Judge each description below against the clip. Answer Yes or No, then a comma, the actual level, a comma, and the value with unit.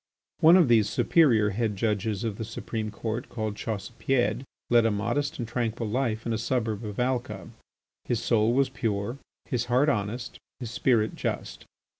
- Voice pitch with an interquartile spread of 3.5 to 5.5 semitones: No, narrow, 2.4 semitones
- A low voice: Yes, low, 115 Hz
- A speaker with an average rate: Yes, average, 165 wpm